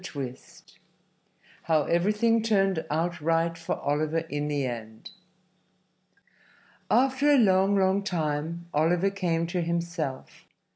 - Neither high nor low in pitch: Yes, medium, 170 Hz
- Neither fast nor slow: No, slow, 110 wpm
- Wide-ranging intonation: No, average, 4.2 semitones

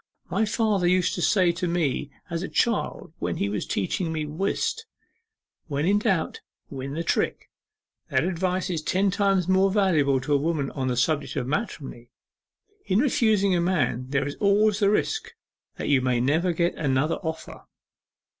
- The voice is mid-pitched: Yes, medium, 170 Hz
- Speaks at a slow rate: No, average, 175 wpm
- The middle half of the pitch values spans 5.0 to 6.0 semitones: Yes, wide, 5.5 semitones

